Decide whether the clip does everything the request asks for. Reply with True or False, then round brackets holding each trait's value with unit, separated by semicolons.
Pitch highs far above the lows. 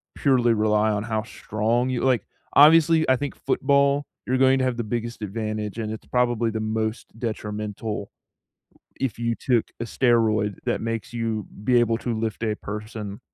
False (2.6 semitones)